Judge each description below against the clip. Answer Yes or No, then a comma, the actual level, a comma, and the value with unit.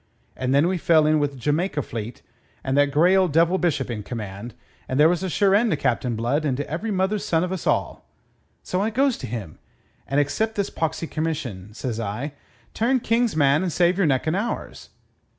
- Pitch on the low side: No, medium, 155 Hz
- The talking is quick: Yes, fast, 215 wpm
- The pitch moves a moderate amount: No, wide, 6.3 semitones